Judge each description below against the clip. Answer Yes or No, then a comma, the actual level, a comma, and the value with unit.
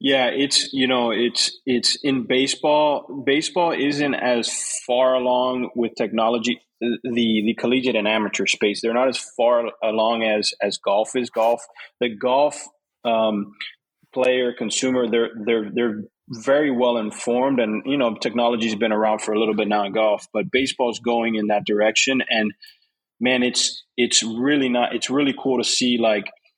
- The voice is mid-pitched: No, low, 120 Hz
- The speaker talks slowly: No, average, 165 wpm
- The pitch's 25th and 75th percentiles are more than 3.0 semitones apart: No, narrow, 2.6 semitones